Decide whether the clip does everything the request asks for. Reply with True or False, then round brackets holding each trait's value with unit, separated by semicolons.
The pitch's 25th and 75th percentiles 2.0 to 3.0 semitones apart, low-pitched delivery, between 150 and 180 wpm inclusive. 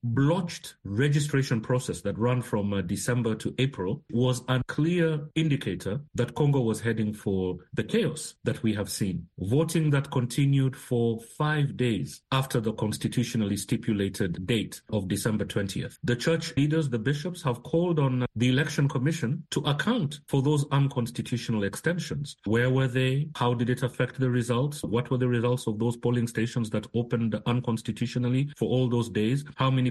False (3.7 semitones; 125 Hz; 165 wpm)